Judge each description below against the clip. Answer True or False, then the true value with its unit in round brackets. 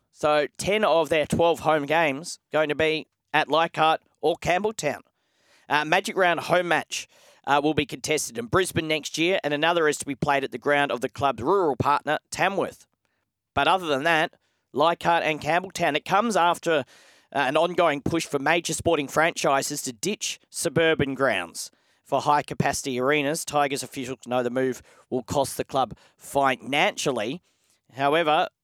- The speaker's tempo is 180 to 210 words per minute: False (165 wpm)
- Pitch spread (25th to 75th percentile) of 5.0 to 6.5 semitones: False (3.1 semitones)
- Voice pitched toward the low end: False (155 Hz)